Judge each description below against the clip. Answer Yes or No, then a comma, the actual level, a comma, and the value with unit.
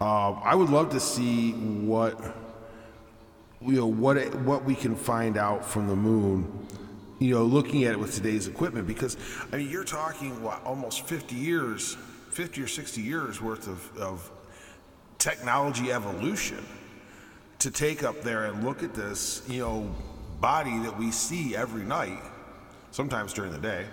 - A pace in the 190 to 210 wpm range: No, average, 165 wpm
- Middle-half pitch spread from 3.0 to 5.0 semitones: Yes, average, 3.8 semitones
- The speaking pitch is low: Yes, low, 115 Hz